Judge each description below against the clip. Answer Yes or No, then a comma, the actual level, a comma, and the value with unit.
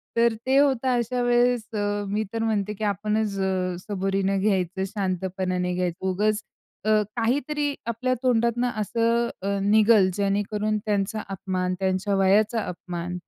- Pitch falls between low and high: No, high, 205 Hz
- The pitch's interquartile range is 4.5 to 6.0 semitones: No, average, 3.3 semitones